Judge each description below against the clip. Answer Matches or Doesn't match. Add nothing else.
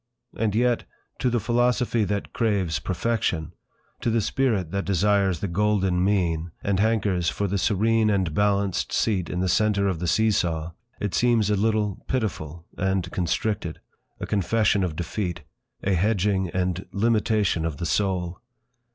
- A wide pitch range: Doesn't match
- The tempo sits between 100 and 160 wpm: Matches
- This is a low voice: Matches